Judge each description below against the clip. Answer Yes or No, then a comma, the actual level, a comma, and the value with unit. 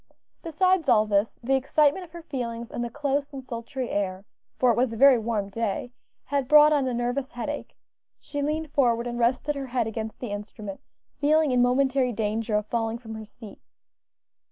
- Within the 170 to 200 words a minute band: Yes, average, 190 wpm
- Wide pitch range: No, average, 3.9 semitones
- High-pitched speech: Yes, high, 245 Hz